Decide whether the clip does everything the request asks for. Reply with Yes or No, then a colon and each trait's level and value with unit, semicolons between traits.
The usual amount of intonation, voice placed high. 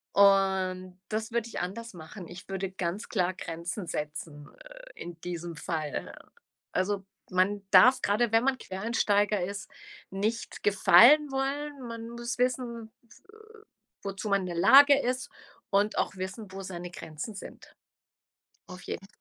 Yes: average, 4.3 semitones; high, 200 Hz